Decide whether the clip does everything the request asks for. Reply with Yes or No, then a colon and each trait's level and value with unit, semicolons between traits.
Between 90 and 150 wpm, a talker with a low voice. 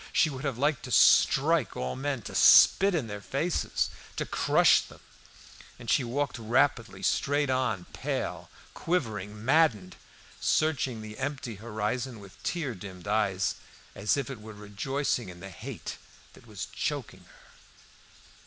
Yes: average, 145 wpm; low, 120 Hz